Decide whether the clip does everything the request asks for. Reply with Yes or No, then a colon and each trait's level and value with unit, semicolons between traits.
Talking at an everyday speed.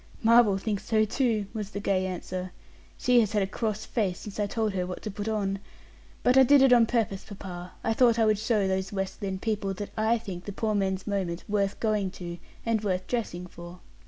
No: fast, 220 wpm